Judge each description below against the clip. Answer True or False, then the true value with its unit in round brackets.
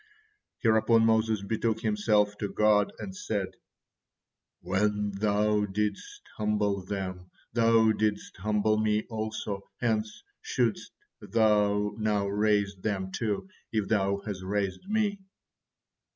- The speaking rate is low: True (110 wpm)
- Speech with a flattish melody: True (1.4 semitones)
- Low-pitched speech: True (105 Hz)